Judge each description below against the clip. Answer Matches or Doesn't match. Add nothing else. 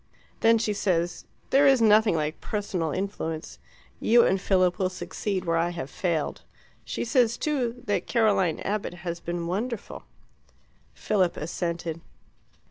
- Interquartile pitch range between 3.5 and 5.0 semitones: Matches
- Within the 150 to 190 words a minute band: Doesn't match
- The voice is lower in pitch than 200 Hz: Matches